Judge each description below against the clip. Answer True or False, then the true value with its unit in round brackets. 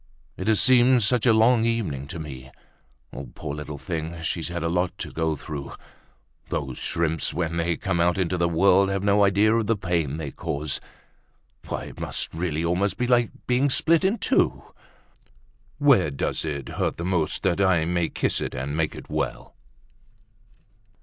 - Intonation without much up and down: False (4.9 semitones)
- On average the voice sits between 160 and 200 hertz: False (85 Hz)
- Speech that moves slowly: False (175 wpm)